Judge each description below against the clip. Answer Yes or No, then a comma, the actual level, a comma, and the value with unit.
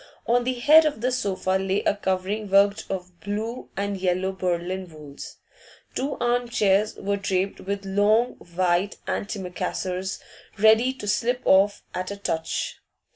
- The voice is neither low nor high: No, high, 200 Hz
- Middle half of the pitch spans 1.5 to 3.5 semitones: Yes, average, 2.8 semitones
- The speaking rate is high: No, average, 145 wpm